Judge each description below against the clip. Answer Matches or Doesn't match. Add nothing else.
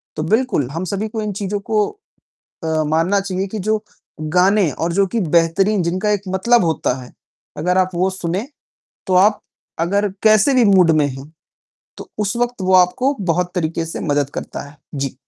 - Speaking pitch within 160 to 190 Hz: Matches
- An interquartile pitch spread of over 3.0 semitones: Matches